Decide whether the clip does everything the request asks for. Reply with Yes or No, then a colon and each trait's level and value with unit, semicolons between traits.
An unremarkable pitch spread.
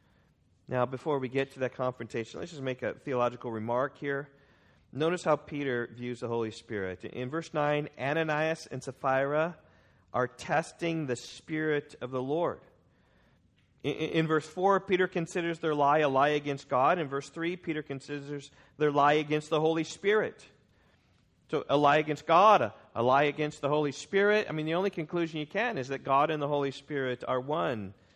Yes: average, 3.6 semitones